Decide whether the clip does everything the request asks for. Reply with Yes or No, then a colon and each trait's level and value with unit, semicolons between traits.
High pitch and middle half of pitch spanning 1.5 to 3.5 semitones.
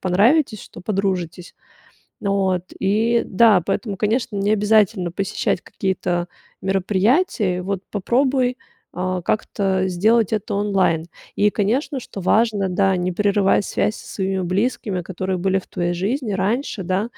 Yes: high, 195 Hz; average, 2.7 semitones